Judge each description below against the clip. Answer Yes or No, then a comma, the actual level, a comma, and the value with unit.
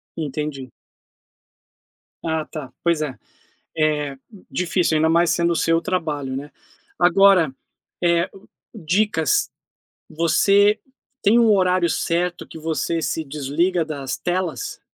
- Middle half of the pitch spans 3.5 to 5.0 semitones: No, average, 2.9 semitones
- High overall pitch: No, medium, 165 Hz